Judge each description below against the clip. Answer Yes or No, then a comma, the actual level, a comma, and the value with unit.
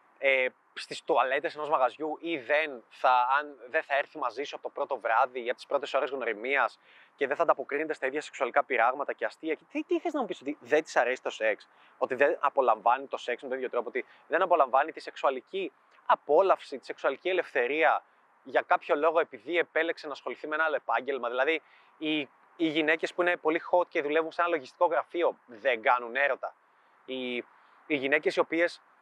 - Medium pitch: Yes, medium, 160 Hz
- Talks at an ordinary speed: No, fast, 205 wpm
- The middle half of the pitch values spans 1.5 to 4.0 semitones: Yes, average, 3.0 semitones